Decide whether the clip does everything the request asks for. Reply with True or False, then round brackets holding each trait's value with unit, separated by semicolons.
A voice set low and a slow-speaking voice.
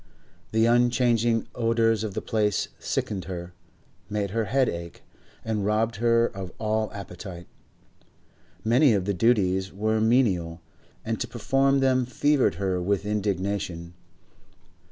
True (105 Hz; 130 wpm)